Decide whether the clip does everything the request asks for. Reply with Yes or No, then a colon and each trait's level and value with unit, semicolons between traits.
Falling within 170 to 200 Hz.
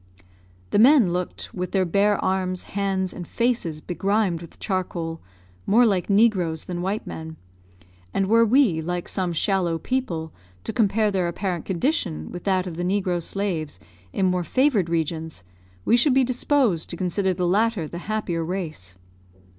Yes: medium, 185 Hz